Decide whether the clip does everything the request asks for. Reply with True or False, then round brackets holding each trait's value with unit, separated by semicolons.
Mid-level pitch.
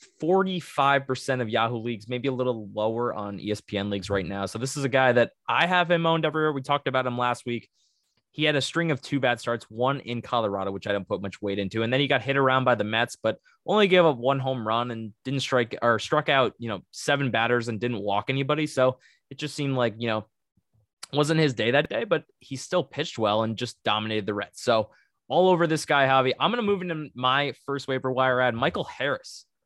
False (130 Hz)